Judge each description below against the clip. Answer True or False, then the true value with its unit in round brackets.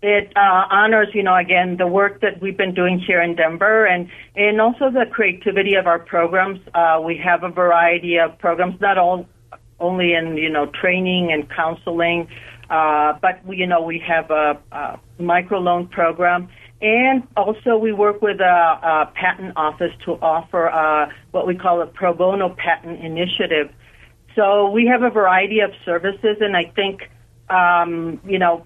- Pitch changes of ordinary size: True (3.0 semitones)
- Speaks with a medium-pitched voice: True (180 Hz)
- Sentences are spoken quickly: False (170 wpm)